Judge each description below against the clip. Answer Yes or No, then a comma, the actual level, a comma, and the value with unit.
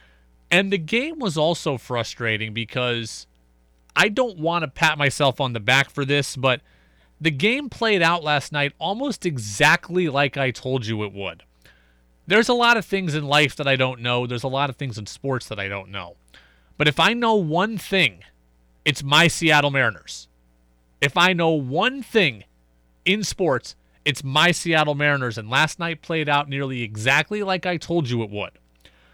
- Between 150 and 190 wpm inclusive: Yes, average, 185 wpm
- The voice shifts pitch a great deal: Yes, wide, 8.4 semitones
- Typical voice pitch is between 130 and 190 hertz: Yes, medium, 140 Hz